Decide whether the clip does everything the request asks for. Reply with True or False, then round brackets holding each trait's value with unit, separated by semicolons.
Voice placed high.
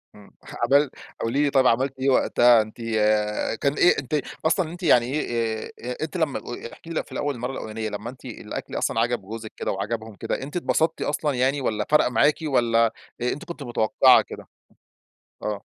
False (125 Hz)